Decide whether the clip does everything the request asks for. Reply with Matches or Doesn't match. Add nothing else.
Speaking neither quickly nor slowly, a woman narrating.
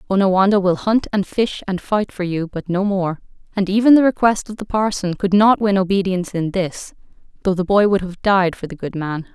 Doesn't match